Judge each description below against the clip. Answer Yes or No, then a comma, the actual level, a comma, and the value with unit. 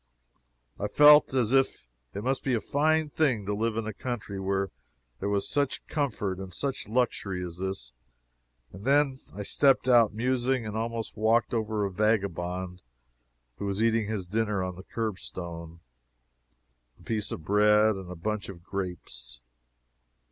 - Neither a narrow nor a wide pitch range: Yes, average, 4.0 semitones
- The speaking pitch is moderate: No, low, 105 Hz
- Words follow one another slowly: No, average, 160 wpm